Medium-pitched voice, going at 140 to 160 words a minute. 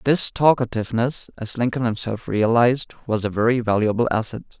No: low, 115 Hz; average, 145 wpm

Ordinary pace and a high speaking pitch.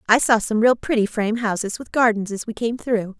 No: fast, 245 wpm; high, 225 Hz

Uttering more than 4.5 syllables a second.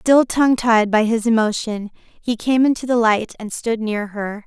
No: 4.4 syllables/s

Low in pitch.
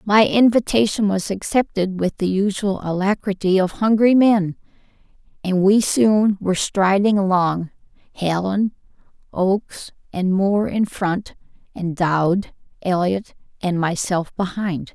No: high, 195 Hz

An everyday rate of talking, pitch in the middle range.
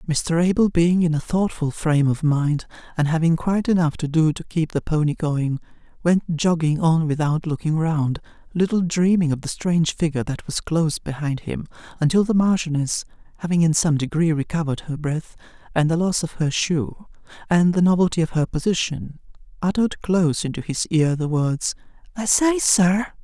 Yes: average, 175 wpm; medium, 165 Hz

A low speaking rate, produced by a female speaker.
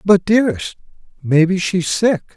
No: slow, 125 wpm; male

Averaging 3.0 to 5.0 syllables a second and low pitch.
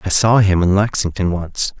Yes: 4.9 syllables/s; very low, 95 Hz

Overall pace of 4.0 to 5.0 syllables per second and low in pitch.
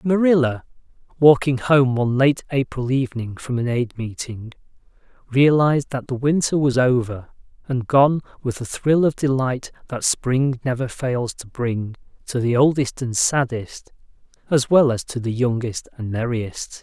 Yes: 4.4 syllables/s; low, 130 Hz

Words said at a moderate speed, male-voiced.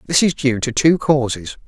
No: fast, 215 wpm; male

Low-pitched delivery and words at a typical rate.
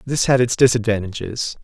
Yes: low, 115 Hz; average, 145 wpm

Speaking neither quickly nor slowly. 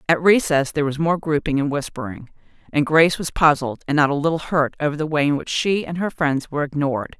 No: fast, 235 wpm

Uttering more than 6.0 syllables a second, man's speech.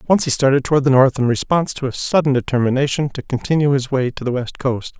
Yes: 6.4 syllables/s; male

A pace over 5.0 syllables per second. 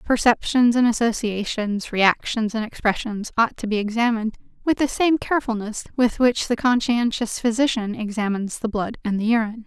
Yes: 5.3 syllables/s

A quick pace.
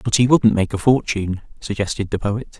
Yes: fast, 210 wpm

